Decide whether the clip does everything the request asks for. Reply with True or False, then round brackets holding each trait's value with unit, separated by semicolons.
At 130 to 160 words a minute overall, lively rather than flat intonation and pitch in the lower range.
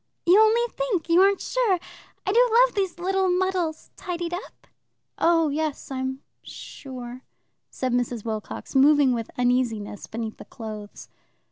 False (140 wpm; 7.4 semitones; 315 Hz)